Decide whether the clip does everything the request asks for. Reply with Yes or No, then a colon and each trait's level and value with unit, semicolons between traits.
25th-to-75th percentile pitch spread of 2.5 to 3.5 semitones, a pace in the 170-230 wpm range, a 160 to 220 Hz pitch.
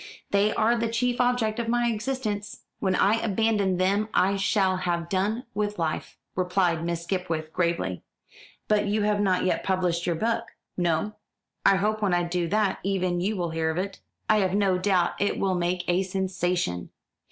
Yes: average, 3.1 semitones; average, 180 wpm; high, 190 Hz